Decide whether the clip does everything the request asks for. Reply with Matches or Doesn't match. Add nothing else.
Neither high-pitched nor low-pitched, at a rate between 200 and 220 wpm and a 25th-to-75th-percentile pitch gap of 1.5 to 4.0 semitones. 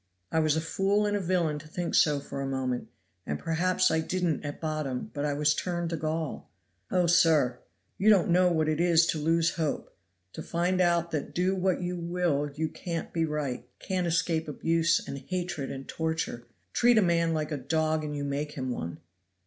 Matches